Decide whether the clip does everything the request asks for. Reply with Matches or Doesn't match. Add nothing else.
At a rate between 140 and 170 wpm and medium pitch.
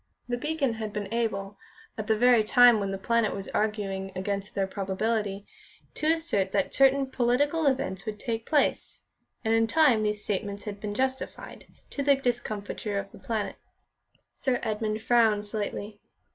Doesn't match